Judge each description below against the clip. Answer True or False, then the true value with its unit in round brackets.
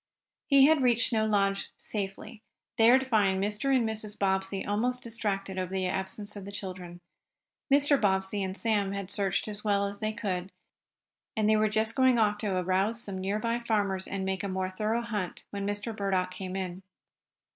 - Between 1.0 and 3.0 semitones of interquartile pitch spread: True (2.4 semitones)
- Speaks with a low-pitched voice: False (205 Hz)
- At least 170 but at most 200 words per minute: True (185 wpm)